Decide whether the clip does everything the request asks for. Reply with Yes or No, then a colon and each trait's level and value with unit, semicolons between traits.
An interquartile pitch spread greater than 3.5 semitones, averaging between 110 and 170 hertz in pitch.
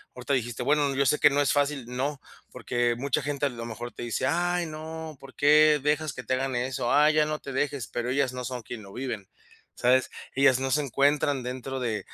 No: average, 2.9 semitones; low, 135 Hz